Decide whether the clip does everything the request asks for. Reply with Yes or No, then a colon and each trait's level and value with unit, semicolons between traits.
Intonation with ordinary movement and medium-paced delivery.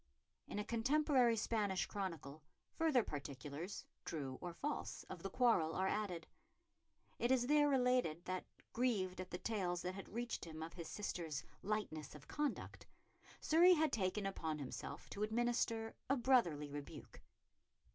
No: wide, 6.5 semitones; average, 145 wpm